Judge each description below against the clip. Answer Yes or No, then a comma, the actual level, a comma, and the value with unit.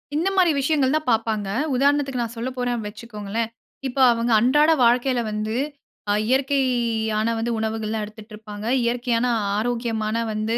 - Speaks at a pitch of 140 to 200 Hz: No, high, 230 Hz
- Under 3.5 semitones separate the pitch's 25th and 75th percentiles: Yes, average, 2.8 semitones